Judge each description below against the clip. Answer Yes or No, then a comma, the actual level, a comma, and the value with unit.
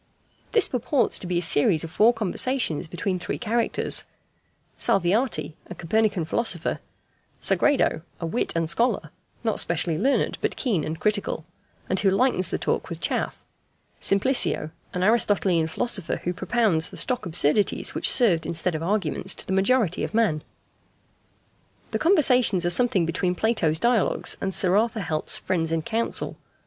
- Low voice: No, high, 190 Hz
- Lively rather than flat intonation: Yes, wide, 5.7 semitones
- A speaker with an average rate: Yes, average, 155 wpm